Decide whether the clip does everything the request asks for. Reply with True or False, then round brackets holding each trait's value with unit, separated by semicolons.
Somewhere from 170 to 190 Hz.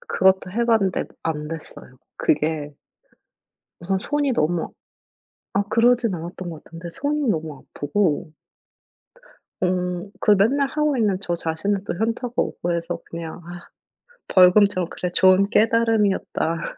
True (185 Hz)